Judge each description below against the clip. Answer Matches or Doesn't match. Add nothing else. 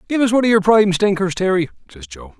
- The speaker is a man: Matches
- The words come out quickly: Matches